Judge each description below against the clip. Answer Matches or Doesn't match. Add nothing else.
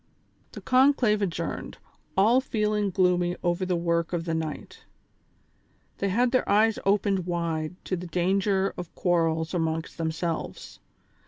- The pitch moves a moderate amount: Matches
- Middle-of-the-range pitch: Matches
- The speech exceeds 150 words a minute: Doesn't match